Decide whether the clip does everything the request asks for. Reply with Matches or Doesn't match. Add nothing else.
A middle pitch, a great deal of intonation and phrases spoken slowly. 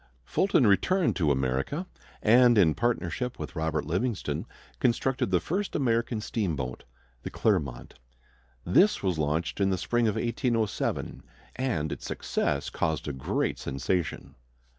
Doesn't match